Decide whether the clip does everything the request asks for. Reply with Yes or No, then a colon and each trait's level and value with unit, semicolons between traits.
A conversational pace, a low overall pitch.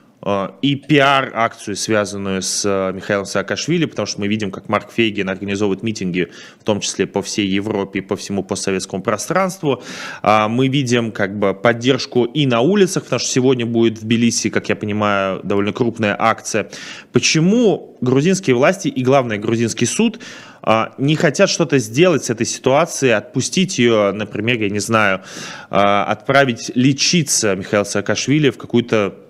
Yes: average, 145 wpm; low, 115 Hz